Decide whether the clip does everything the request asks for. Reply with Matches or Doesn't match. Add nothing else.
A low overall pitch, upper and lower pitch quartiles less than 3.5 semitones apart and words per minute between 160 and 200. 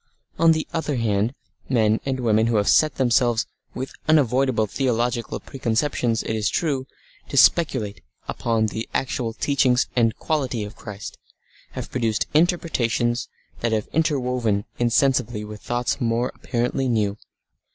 Doesn't match